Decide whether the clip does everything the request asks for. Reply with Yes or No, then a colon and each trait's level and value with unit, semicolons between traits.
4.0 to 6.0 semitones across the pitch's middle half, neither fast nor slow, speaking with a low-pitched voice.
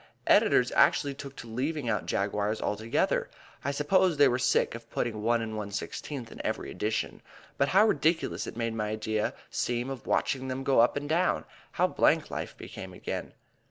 Yes: average, 4.5 semitones; average, 175 wpm; low, 120 Hz